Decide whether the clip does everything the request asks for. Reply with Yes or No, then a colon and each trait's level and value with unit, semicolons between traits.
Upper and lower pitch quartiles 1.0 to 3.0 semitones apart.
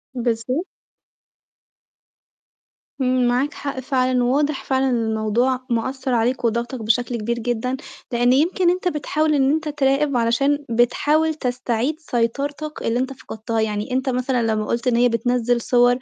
Yes: average, 2.7 semitones